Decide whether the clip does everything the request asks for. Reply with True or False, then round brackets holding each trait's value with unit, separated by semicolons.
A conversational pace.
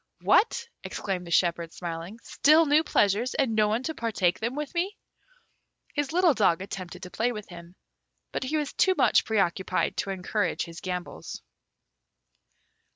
True (160 wpm)